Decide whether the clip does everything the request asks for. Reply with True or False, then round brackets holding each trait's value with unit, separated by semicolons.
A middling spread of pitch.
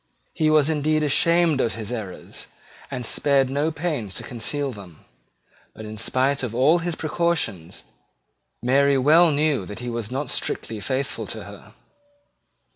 True (4.8 semitones)